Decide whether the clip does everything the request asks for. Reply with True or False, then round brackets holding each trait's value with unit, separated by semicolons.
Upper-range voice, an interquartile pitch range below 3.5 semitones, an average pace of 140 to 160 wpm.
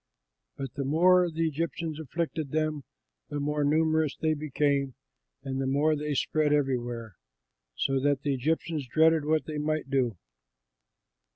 False (150 Hz; 2.5 semitones; 145 wpm)